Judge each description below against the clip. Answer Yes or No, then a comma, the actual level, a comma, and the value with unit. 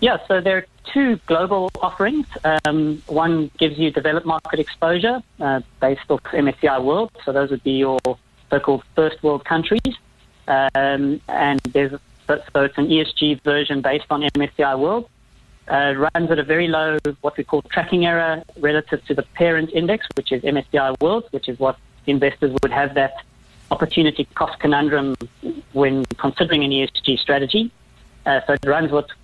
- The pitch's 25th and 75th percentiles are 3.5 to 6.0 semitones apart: No, average, 2.8 semitones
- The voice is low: No, medium, 150 Hz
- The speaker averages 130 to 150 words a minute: No, average, 170 wpm